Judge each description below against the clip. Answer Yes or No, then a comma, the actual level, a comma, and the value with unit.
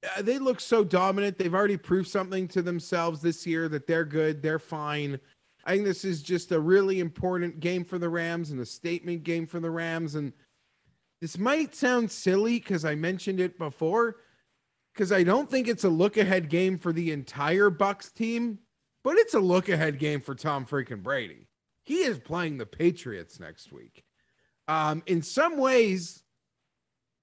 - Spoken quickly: No, average, 180 wpm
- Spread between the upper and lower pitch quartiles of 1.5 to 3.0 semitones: No, average, 3.7 semitones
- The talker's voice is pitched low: No, medium, 175 Hz